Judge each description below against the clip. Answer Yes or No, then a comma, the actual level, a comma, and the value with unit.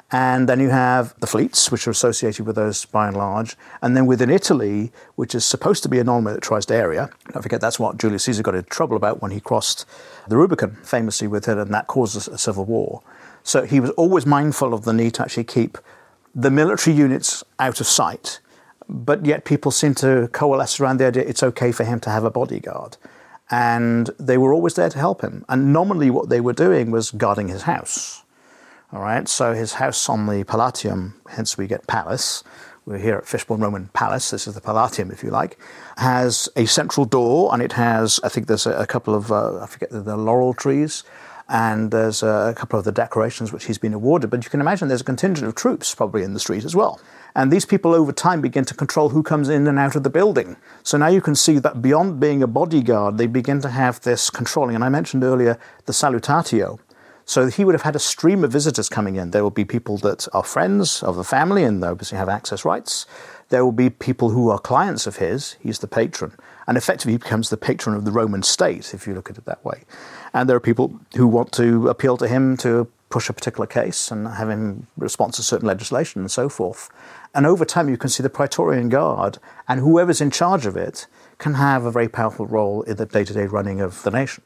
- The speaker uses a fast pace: Yes, fast, 230 wpm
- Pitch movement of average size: Yes, average, 4.1 semitones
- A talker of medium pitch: No, low, 120 Hz